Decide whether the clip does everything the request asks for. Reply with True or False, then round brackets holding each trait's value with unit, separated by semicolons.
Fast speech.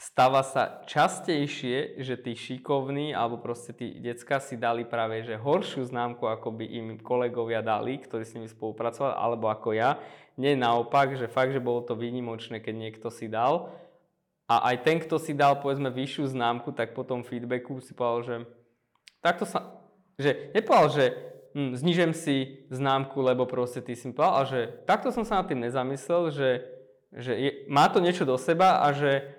True (180 wpm)